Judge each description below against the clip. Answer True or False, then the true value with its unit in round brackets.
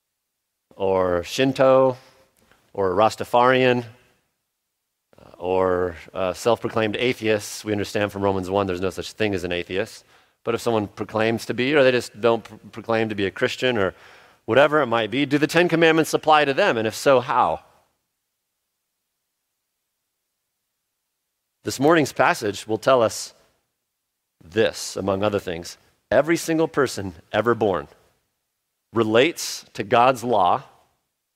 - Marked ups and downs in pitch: False (4.8 semitones)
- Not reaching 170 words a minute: True (135 wpm)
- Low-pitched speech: True (115 Hz)